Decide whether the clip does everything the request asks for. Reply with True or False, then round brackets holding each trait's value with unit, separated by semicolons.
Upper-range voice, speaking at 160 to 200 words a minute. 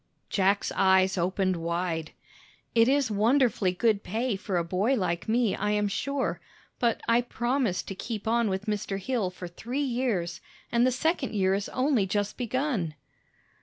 True (210 Hz; 165 wpm)